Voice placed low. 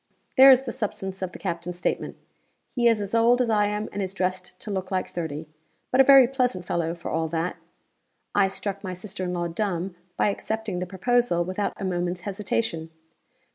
No: high, 190 Hz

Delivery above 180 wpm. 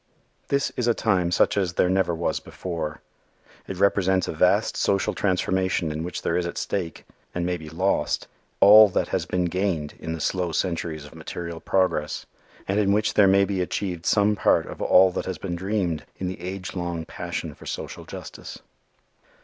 Yes: average, 190 wpm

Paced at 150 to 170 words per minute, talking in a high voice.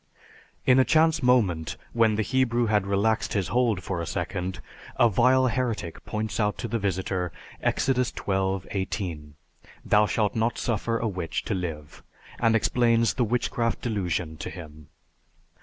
No: average, 155 wpm; low, 105 Hz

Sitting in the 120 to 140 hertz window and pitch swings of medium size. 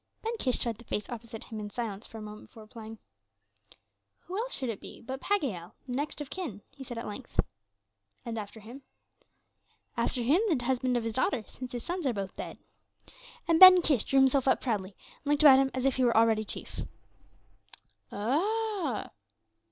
No: very high, 250 Hz; average, 4.3 semitones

